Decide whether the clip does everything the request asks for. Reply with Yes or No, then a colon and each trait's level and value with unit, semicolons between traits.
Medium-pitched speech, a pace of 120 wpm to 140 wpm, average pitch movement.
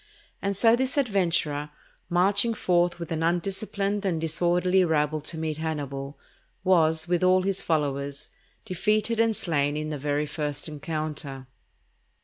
Yes: medium, 165 Hz; slow, 135 wpm; average, 4.2 semitones